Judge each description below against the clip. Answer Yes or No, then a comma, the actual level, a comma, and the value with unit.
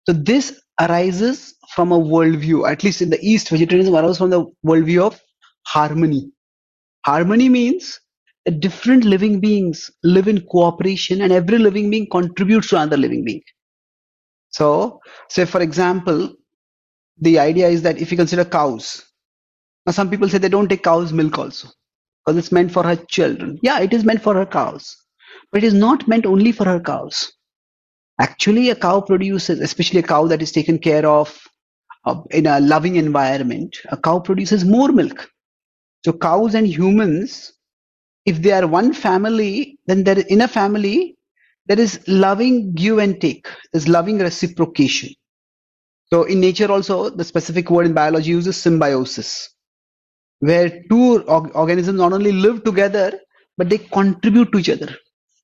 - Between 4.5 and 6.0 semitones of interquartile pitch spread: No, average, 4.0 semitones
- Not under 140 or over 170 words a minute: Yes, average, 160 wpm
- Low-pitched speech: No, medium, 185 Hz